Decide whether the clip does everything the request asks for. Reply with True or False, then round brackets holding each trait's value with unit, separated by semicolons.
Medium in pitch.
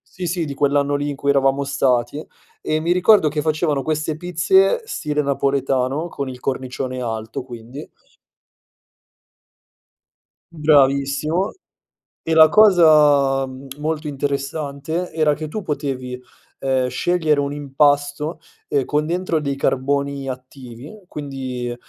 True (145 Hz)